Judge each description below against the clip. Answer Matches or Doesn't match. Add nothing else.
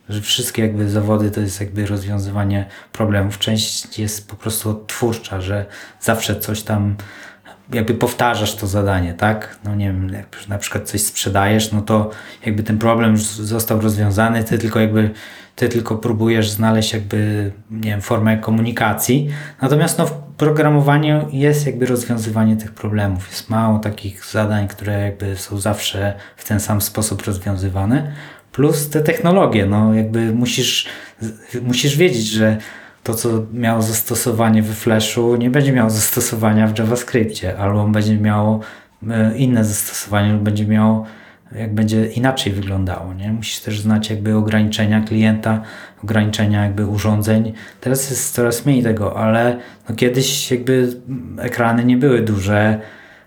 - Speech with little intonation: Matches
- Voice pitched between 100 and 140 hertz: Matches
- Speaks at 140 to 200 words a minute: Matches